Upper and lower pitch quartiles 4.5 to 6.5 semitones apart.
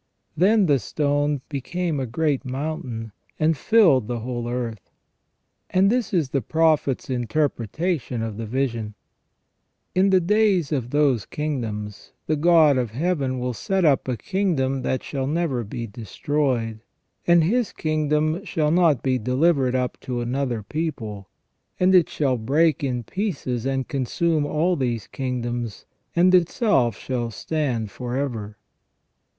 Yes: average, 5.1 semitones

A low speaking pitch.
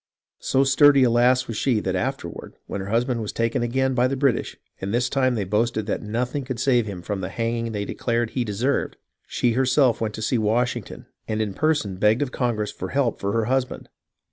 Yes: low, 120 Hz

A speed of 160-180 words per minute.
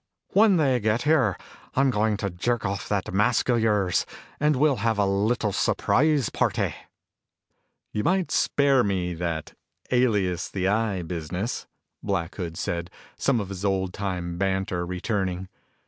No: average, 150 wpm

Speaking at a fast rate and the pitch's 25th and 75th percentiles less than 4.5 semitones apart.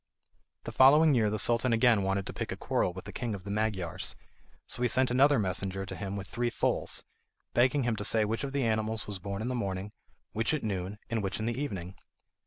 Yes: fast, 230 wpm; average, 3.8 semitones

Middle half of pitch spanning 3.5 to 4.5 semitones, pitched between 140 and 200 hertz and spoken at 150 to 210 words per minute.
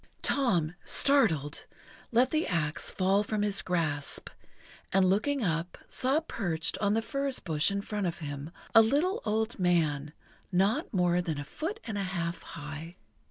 No: wide, 5.5 semitones; high, 190 Hz; average, 160 wpm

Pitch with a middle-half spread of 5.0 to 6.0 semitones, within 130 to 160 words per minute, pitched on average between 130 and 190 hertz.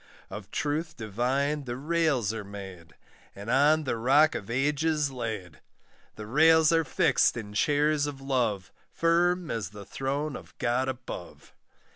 Yes: wide, 5.6 semitones; average, 145 wpm; low, 135 Hz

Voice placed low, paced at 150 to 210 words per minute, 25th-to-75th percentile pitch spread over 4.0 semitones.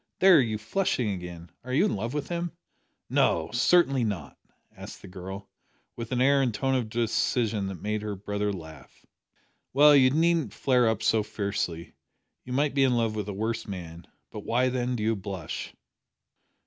Yes: low, 115 Hz; average, 180 wpm; average, 4.7 semitones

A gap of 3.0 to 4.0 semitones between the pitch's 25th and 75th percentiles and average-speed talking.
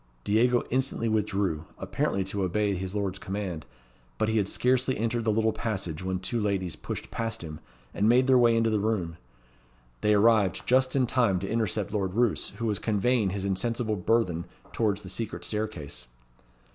Yes: average, 3.3 semitones; average, 175 wpm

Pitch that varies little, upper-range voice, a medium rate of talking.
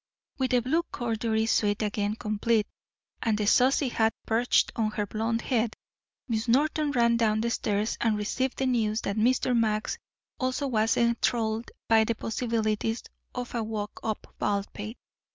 Yes: narrow, 2.1 semitones; high, 225 Hz; average, 155 wpm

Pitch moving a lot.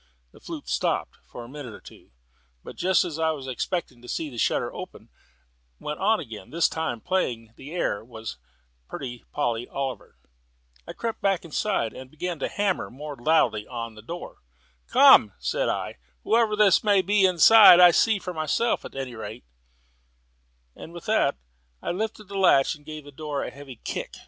Yes: wide, 7.2 semitones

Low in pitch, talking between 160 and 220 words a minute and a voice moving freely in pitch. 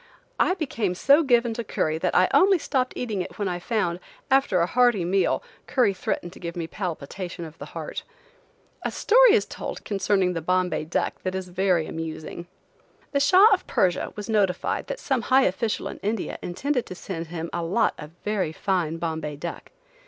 No: high, 190 Hz; average, 190 wpm; wide, 5.9 semitones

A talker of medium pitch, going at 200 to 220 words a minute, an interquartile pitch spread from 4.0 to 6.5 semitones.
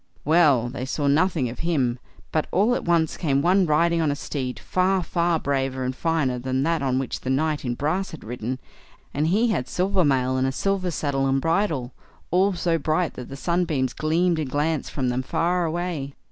Yes: medium, 155 Hz; fast, 205 wpm; average, 4.6 semitones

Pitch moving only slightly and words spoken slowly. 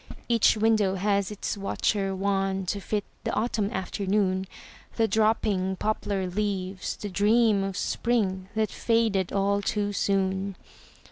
Yes: narrow, 1.8 semitones; slow, 130 wpm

